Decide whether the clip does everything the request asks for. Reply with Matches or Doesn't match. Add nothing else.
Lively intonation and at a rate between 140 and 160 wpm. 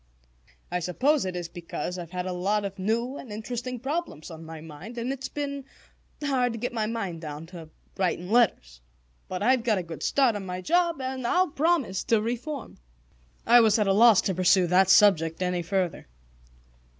Doesn't match